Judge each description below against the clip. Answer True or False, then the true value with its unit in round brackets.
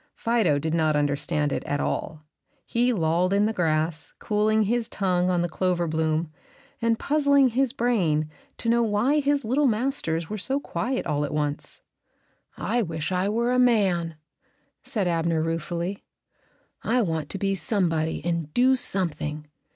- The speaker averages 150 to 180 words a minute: True (160 wpm)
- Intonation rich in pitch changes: True (6.5 semitones)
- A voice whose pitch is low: False (185 Hz)